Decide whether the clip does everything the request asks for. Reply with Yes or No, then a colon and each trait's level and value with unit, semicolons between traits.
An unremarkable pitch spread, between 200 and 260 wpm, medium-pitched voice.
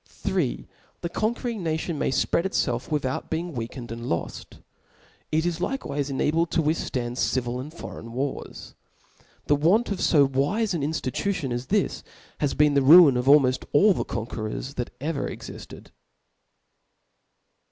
No: average, 4.7 semitones; average, 150 wpm; medium, 145 Hz